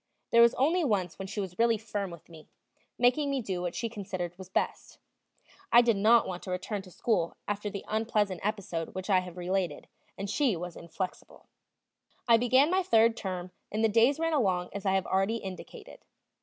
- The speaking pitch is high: Yes, high, 200 Hz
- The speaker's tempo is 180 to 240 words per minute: Yes, average, 195 wpm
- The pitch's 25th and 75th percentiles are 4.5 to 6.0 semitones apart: No, average, 4.0 semitones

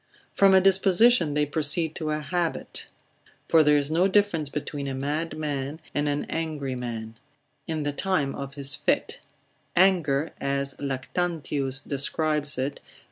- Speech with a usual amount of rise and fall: Yes, average, 3.1 semitones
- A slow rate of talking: No, average, 150 wpm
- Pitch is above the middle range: No, medium, 150 Hz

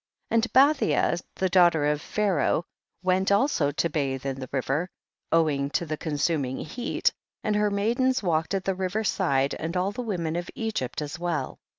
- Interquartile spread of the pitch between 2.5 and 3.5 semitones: No, wide, 5.5 semitones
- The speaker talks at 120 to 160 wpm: No, average, 180 wpm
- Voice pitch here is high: No, medium, 175 Hz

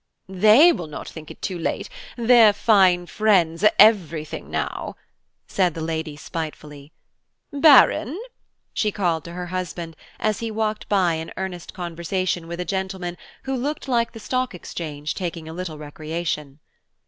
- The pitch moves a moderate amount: Yes, average, 4.7 semitones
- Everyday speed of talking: Yes, average, 150 wpm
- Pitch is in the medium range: Yes, medium, 180 Hz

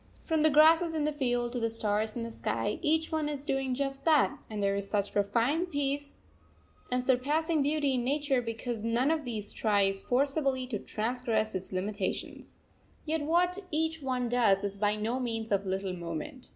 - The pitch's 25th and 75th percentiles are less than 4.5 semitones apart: No, wide, 5.5 semitones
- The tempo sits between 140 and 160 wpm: No, average, 185 wpm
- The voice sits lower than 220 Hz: No, very high, 250 Hz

